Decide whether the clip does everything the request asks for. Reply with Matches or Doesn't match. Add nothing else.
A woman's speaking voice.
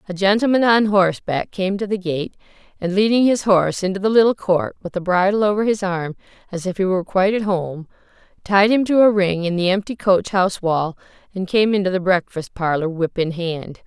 Matches